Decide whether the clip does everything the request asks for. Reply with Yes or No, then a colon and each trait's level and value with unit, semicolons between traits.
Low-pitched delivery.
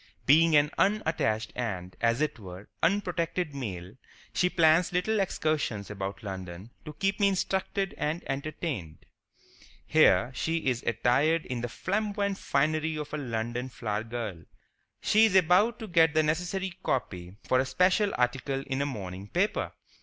No: medium, 150 Hz